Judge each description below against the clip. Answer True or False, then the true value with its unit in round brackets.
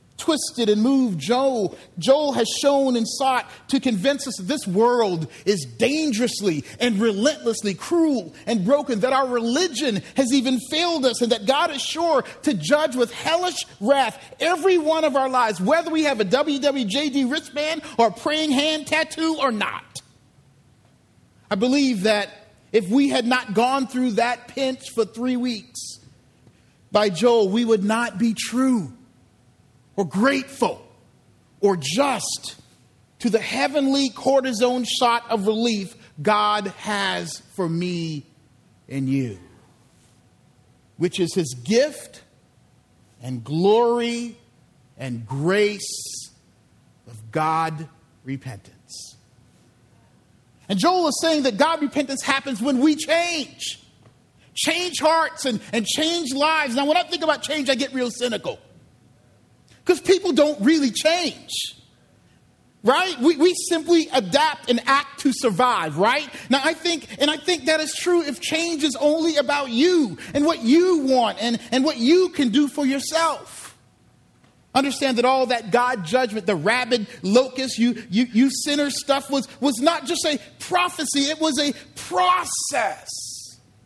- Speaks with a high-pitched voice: True (255 Hz)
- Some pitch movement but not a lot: False (6.6 semitones)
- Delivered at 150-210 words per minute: False (140 wpm)